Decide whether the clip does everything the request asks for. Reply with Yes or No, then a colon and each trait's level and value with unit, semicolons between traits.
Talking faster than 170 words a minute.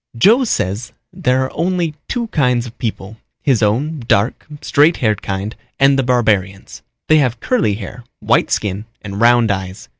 No: average, 160 wpm